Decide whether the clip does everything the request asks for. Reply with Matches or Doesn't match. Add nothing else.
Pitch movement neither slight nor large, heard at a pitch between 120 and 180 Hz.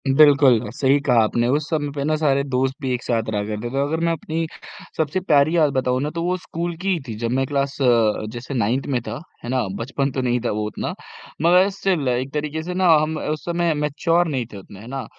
Matches